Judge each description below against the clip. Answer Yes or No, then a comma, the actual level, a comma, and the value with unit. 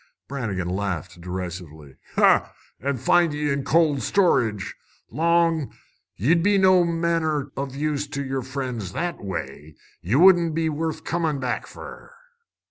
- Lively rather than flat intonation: Yes, wide, 7.6 semitones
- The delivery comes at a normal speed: No, slow, 130 wpm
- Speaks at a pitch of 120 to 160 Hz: Yes, medium, 140 Hz